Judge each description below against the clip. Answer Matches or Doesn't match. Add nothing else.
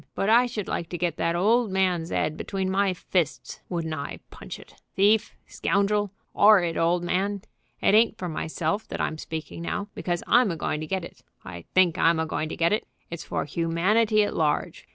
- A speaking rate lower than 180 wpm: Doesn't match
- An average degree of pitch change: Matches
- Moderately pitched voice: Matches